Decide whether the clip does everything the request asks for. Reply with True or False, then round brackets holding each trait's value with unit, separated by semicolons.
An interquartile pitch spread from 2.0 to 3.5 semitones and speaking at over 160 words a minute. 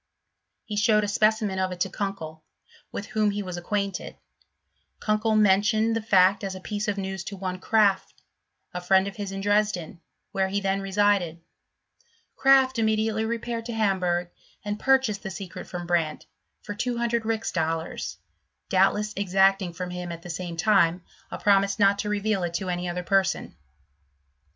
True (2.7 semitones; 175 wpm)